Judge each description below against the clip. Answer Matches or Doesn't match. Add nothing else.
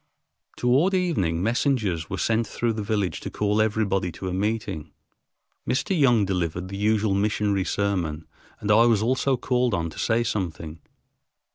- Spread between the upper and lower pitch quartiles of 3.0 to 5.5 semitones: Matches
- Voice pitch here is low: Matches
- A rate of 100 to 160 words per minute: Matches